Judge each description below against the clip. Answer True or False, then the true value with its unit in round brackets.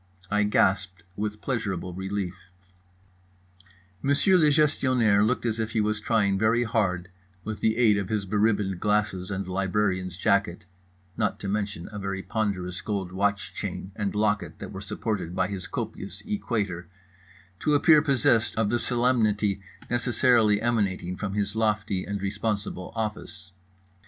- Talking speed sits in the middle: True (145 wpm)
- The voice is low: True (105 Hz)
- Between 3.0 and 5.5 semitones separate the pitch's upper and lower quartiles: False (2.6 semitones)